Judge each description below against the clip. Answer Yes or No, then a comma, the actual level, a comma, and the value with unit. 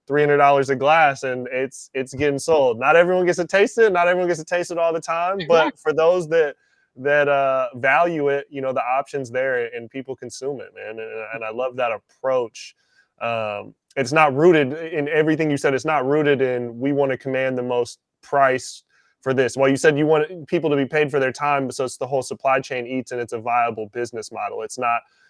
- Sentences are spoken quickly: Yes, fast, 230 wpm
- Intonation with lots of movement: No, average, 3.8 semitones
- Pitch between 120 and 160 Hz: Yes, medium, 140 Hz